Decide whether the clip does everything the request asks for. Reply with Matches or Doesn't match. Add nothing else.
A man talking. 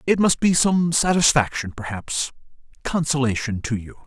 Matches